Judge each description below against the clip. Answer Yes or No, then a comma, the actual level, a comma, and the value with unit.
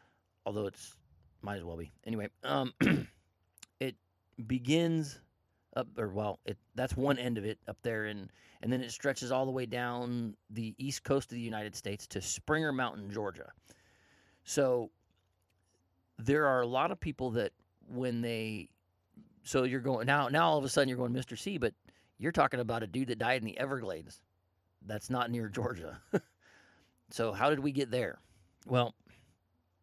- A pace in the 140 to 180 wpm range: Yes, average, 175 wpm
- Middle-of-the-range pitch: No, low, 115 Hz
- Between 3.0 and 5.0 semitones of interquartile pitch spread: Yes, average, 4.5 semitones